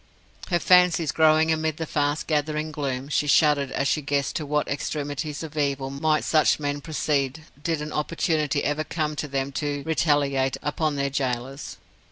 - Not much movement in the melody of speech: Yes, narrow, 1.8 semitones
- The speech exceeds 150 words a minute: Yes, average, 170 wpm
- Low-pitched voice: No, medium, 150 Hz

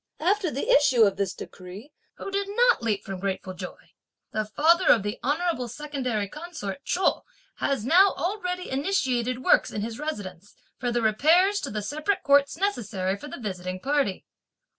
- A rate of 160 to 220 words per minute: Yes, average, 165 wpm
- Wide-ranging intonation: Yes, wide, 8.4 semitones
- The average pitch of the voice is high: Yes, very high, 260 Hz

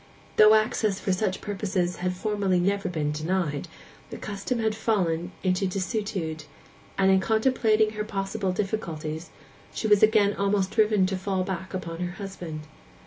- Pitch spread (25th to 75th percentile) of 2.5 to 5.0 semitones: Yes, average, 2.8 semitones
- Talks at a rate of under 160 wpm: Yes, average, 150 wpm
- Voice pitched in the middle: No, high, 195 Hz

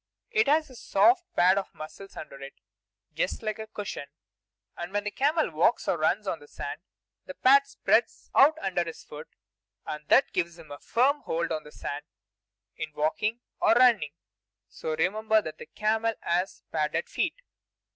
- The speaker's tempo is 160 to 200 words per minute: Yes, average, 175 wpm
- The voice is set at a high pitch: Yes, high, 205 Hz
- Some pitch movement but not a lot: No, wide, 7.9 semitones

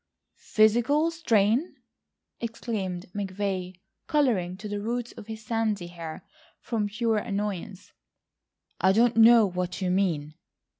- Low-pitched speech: No, high, 210 Hz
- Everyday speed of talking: No, slow, 115 wpm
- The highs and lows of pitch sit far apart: No, average, 3.7 semitones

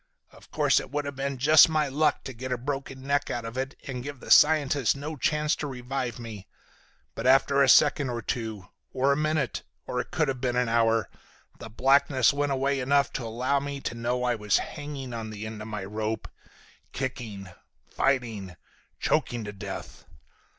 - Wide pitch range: No, average, 3.5 semitones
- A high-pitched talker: No, low, 130 Hz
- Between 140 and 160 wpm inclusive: No, average, 190 wpm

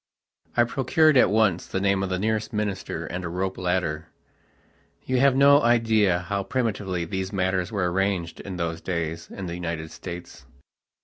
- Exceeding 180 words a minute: No, average, 165 wpm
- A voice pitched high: No, very low, 95 Hz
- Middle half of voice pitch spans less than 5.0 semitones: Yes, average, 3.8 semitones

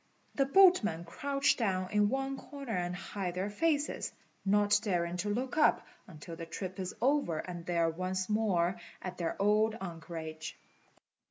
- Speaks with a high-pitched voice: Yes, high, 195 Hz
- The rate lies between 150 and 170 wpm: Yes, average, 160 wpm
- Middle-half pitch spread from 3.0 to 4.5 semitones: No, average, 5.1 semitones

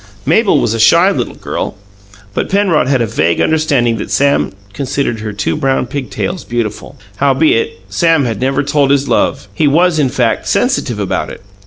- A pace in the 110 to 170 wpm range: No, average, 180 wpm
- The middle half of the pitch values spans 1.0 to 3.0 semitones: No, average, 4.6 semitones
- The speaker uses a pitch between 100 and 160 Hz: Yes, medium, 140 Hz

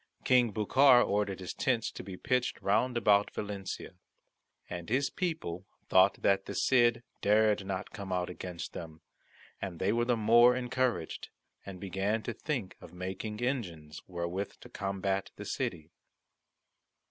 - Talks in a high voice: No, low, 100 Hz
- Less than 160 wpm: Yes, average, 145 wpm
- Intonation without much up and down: No, average, 4.3 semitones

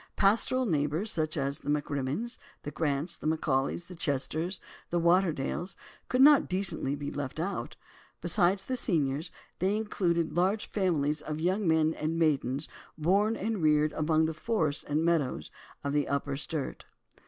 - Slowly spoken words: No, average, 155 wpm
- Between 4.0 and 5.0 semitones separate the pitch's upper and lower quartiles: Yes, average, 4.3 semitones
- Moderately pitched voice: Yes, medium, 160 Hz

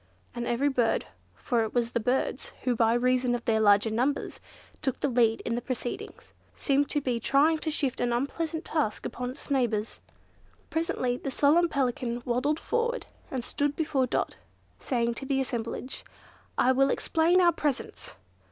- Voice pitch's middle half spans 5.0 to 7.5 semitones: No, average, 3.3 semitones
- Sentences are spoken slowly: No, average, 160 wpm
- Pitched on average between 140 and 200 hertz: No, very high, 255 Hz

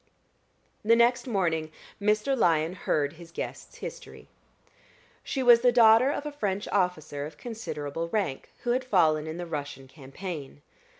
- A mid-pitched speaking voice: Yes, medium, 180 Hz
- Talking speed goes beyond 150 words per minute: No, average, 145 wpm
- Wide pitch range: Yes, wide, 7.1 semitones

